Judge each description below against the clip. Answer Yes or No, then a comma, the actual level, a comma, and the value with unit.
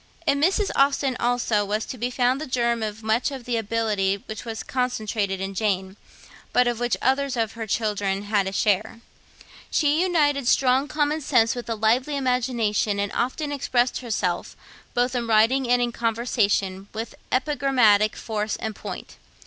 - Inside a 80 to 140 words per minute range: No, average, 165 wpm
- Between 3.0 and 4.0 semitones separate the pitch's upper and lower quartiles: Yes, average, 3.4 semitones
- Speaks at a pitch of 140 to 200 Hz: No, high, 235 Hz